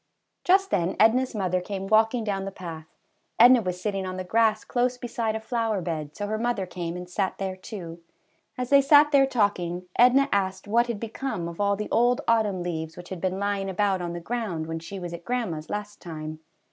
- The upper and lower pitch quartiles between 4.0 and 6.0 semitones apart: Yes, average, 4.4 semitones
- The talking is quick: Yes, fast, 210 wpm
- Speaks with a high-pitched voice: Yes, high, 200 Hz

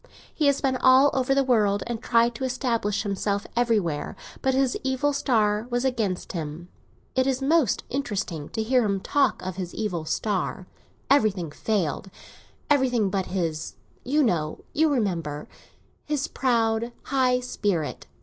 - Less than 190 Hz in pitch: No, high, 230 Hz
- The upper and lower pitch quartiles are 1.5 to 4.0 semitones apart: No, wide, 5.4 semitones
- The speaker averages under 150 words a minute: Yes, average, 140 wpm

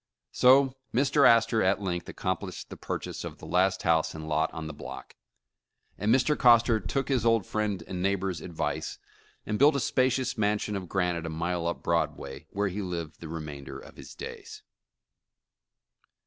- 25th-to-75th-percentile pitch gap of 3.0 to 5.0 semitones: No, wide, 5.6 semitones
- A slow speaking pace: No, average, 170 wpm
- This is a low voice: Yes, very low, 95 Hz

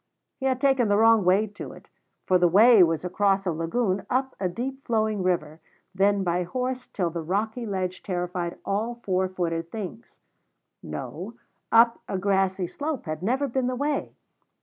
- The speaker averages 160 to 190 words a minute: Yes, average, 170 wpm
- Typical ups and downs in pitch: Yes, average, 4.8 semitones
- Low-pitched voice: No, high, 195 Hz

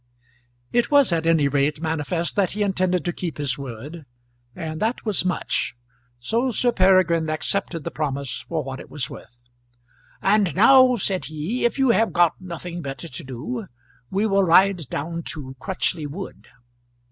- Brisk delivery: No, average, 165 wpm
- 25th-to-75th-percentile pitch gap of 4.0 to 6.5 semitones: Yes, average, 5.1 semitones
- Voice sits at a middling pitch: Yes, medium, 170 Hz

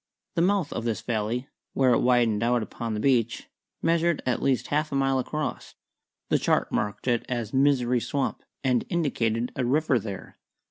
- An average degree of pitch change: Yes, average, 3.4 semitones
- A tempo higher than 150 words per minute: Yes, average, 175 wpm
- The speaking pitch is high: No, low, 125 Hz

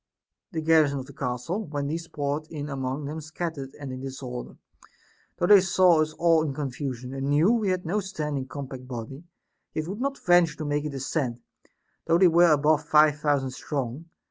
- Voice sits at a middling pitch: Yes, medium, 150 Hz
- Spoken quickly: No, average, 190 wpm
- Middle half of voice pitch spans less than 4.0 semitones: Yes, average, 3.5 semitones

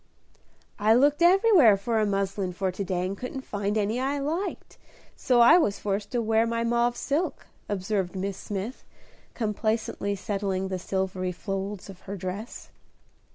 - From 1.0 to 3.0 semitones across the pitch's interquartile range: No, average, 3.6 semitones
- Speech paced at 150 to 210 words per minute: Yes, average, 155 wpm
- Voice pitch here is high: Yes, high, 205 Hz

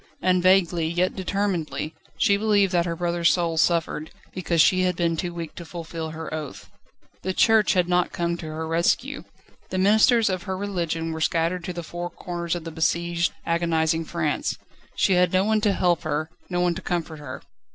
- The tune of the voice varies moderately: No, narrow, 2.1 semitones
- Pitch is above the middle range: No, medium, 175 Hz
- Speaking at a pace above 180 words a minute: Yes, average, 190 wpm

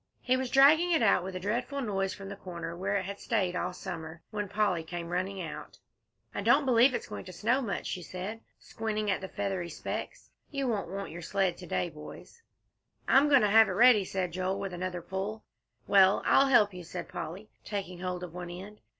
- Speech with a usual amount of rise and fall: Yes, average, 3.4 semitones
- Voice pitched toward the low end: No, high, 195 Hz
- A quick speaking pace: Yes, fast, 215 wpm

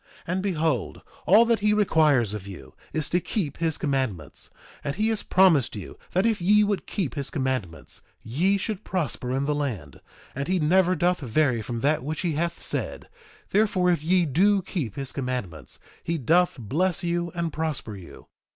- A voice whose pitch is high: No, medium, 155 Hz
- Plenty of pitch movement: Yes, wide, 6.1 semitones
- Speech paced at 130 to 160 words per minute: No, average, 185 wpm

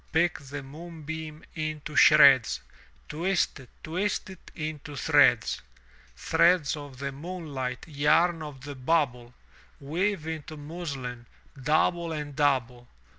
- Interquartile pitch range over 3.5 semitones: No, average, 3.1 semitones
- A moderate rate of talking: No, slow, 115 wpm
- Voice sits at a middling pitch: Yes, medium, 150 Hz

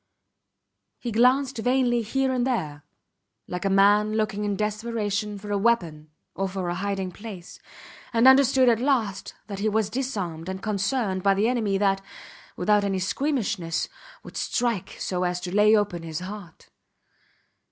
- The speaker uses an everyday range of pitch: Yes, average, 3.6 semitones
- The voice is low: No, high, 205 Hz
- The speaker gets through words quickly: No, average, 155 wpm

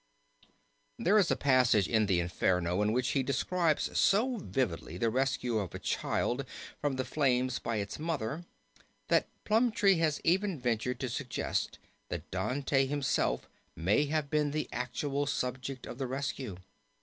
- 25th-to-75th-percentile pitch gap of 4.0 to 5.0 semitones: Yes, average, 4.4 semitones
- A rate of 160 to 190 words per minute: No, average, 150 wpm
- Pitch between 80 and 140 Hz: Yes, low, 135 Hz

